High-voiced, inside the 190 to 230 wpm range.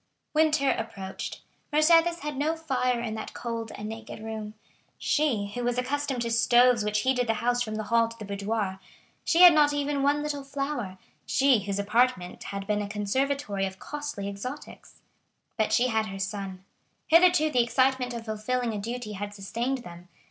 No: high, 235 Hz; average, 170 wpm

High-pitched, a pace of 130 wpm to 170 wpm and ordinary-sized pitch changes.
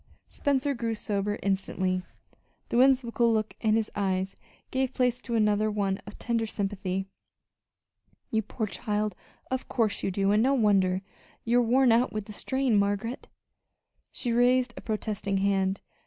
Yes: high, 215 Hz; average, 150 wpm; average, 3.3 semitones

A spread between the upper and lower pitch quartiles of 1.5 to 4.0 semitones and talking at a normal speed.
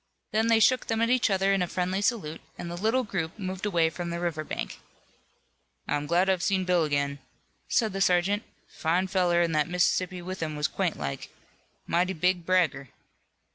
Yes: average, 2.8 semitones; average, 185 wpm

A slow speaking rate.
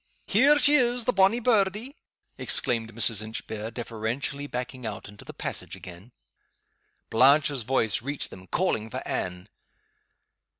Yes: slow, 130 wpm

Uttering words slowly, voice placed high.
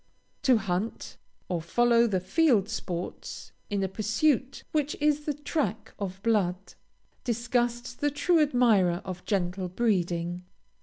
Yes: slow, 125 wpm; high, 220 Hz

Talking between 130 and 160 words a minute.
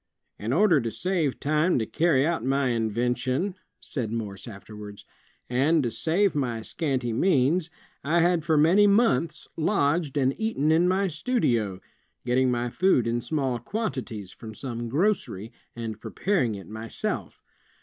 Yes: average, 145 wpm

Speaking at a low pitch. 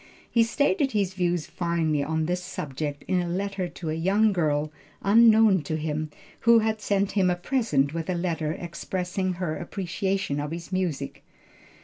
No: medium, 180 Hz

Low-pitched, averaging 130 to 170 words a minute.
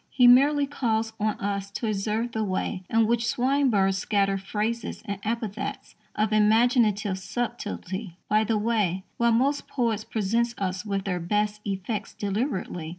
No: high, 215 Hz; average, 150 wpm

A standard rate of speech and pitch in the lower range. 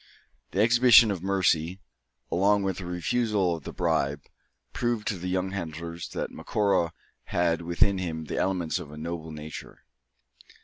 Yes: average, 150 wpm; very low, 90 Hz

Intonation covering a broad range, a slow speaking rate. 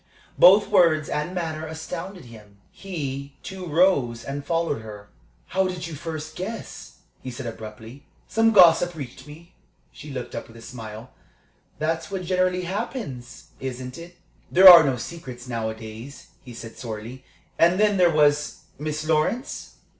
No: wide, 6.1 semitones; average, 150 wpm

